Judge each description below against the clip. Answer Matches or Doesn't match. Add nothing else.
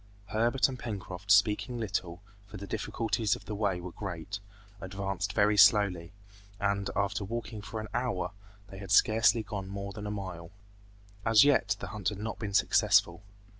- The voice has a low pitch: Matches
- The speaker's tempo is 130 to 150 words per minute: Doesn't match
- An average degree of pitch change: Doesn't match